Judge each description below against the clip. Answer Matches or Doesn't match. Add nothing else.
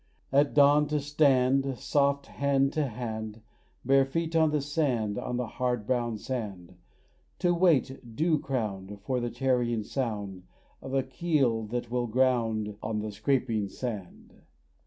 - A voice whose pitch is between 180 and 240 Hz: Doesn't match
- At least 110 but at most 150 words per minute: Matches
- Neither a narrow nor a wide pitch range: Matches